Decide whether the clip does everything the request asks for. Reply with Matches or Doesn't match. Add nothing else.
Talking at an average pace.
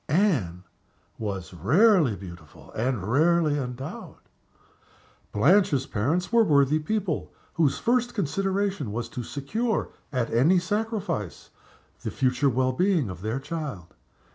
Doesn't match